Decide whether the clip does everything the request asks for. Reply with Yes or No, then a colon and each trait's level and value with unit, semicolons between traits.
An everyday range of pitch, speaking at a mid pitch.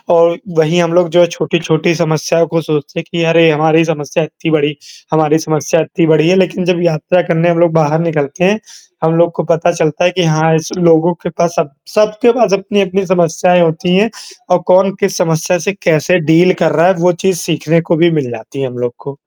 No: narrow, 2.2 semitones; medium, 170 Hz